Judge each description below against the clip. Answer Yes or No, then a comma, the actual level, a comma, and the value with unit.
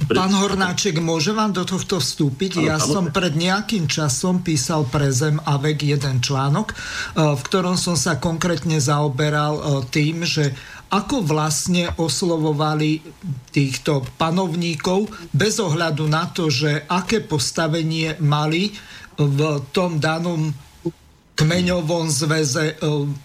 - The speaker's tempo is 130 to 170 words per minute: No, average, 115 wpm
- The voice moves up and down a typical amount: Yes, average, 3.1 semitones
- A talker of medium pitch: Yes, medium, 160 Hz